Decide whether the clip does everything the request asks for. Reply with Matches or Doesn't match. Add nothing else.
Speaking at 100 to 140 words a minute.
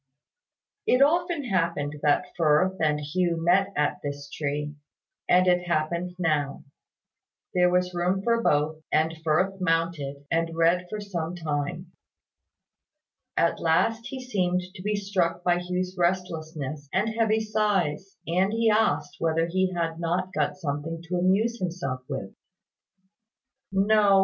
Matches